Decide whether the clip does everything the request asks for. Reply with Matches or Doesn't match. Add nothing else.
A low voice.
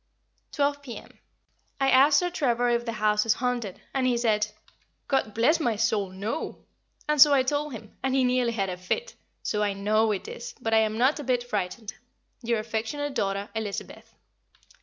Doesn't match